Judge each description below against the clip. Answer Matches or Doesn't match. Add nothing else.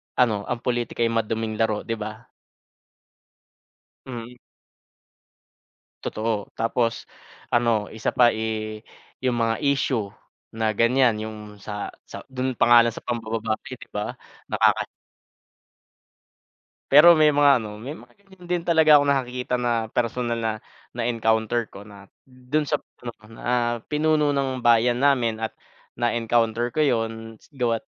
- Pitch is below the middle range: Matches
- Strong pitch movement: Doesn't match